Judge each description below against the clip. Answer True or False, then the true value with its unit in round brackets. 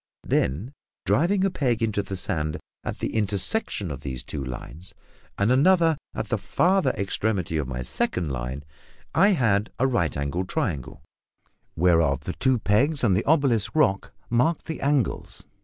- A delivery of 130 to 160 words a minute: True (155 wpm)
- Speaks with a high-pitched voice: False (100 Hz)